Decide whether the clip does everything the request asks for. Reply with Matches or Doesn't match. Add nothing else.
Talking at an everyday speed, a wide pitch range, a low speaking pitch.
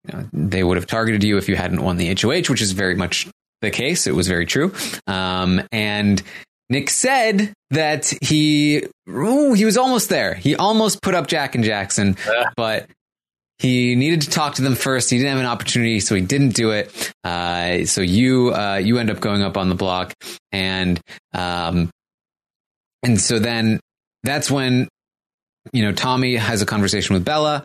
Matches